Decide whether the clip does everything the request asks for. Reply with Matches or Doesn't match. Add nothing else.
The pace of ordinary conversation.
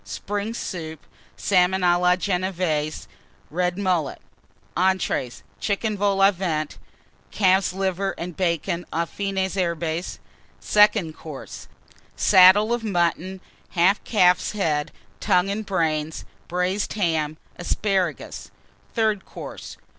Doesn't match